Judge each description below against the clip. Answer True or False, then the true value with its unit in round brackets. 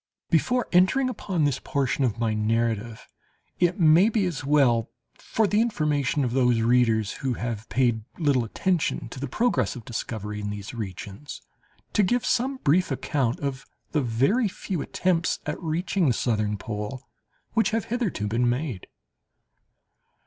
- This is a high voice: False (135 Hz)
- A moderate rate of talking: True (155 wpm)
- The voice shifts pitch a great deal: True (7.7 semitones)